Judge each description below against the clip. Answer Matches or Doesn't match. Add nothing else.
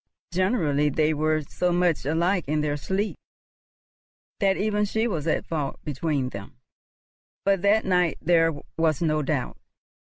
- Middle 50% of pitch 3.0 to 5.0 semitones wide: Matches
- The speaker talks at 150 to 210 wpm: Doesn't match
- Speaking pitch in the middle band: Matches